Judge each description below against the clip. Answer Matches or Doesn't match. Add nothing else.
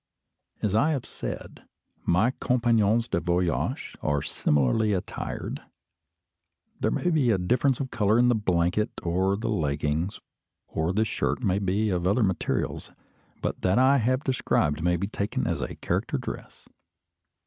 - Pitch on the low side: Matches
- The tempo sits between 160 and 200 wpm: Doesn't match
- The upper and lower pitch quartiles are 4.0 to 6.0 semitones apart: Matches